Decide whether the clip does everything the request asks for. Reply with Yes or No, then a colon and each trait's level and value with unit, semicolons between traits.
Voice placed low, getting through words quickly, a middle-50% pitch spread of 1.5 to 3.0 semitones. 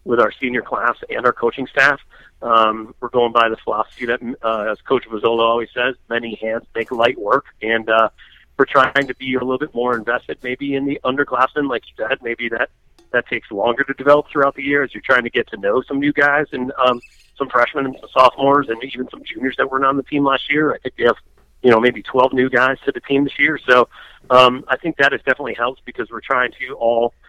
Yes: low, 130 Hz; fast, 240 wpm; average, 2.7 semitones